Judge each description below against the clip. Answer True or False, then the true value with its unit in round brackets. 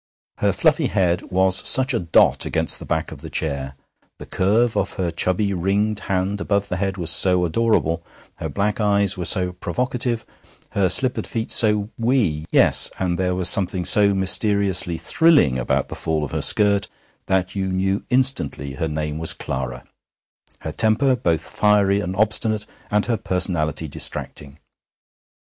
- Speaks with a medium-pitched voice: False (95 Hz)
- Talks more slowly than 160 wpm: False (165 wpm)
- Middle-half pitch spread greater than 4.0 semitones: False (3.5 semitones)